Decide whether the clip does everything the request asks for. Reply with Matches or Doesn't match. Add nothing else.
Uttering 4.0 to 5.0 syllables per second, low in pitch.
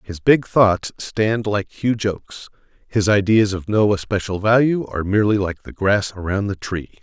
Matches